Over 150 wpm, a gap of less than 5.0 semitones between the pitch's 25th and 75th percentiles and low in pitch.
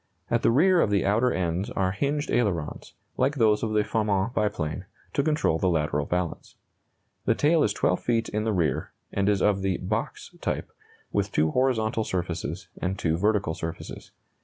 Yes: average, 180 wpm; average, 4.3 semitones; low, 105 Hz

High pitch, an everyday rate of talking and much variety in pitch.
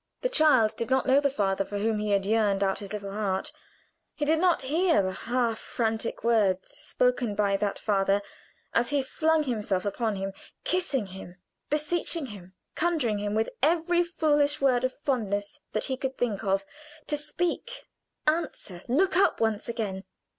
Yes: high, 230 Hz; average, 170 wpm; wide, 6.6 semitones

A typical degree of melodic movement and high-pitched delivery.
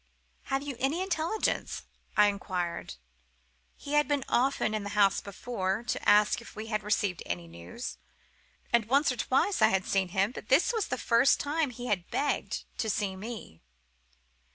No: wide, 5.7 semitones; high, 220 Hz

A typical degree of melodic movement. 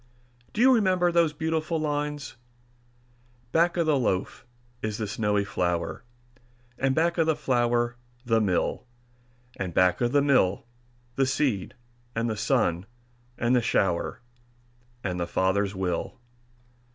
No: wide, 7.2 semitones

